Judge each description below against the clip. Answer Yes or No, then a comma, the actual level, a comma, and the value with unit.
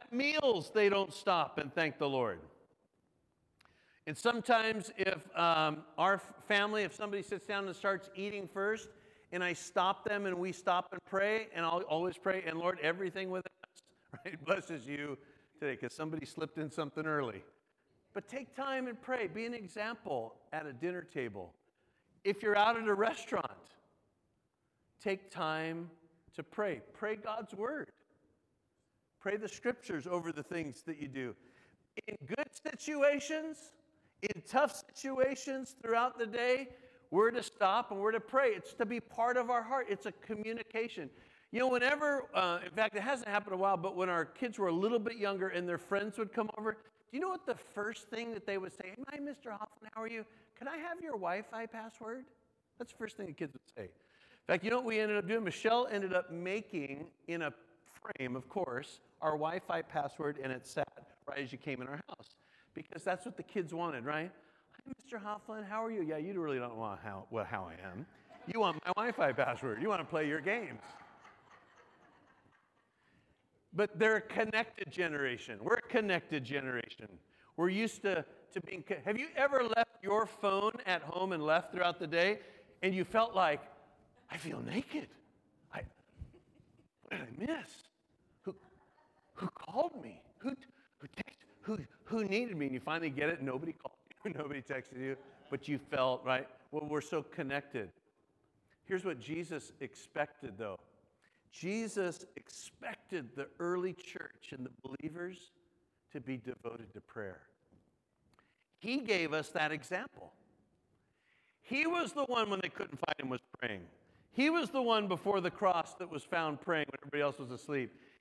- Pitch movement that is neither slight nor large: No, wide, 6.3 semitones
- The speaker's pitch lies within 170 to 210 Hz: Yes, high, 190 Hz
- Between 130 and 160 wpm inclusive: No, average, 180 wpm